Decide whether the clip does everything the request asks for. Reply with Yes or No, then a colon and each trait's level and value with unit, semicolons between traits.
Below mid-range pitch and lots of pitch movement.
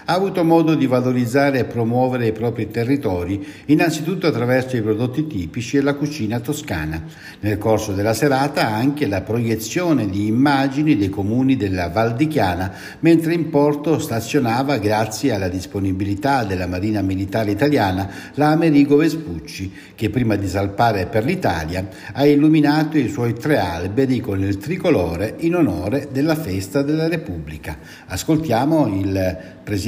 Yes: low, 120 Hz; wide, 6.5 semitones